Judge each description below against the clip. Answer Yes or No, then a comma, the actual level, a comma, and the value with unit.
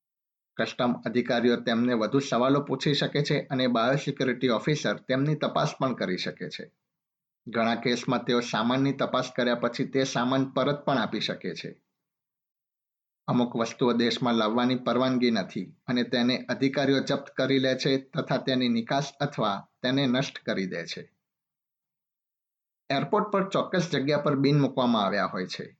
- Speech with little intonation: Yes, narrow, 2.2 semitones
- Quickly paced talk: Yes, fast, 145 wpm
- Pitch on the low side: Yes, low, 130 Hz